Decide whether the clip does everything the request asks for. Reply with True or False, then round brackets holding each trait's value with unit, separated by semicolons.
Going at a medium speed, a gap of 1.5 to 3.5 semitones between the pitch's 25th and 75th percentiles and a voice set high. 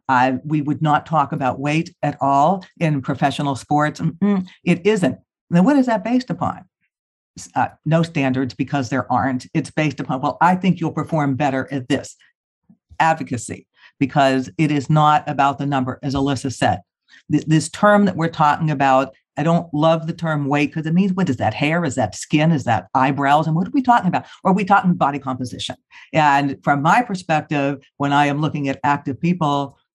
False (195 wpm; 2.9 semitones; 145 Hz)